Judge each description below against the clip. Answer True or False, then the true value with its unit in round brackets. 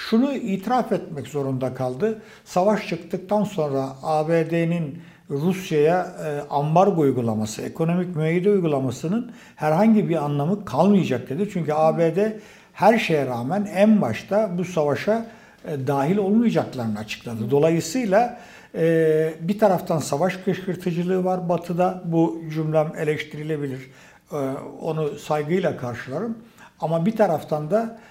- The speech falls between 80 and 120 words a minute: True (105 wpm)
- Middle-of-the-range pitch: True (170 Hz)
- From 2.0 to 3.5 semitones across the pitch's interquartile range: False (5.2 semitones)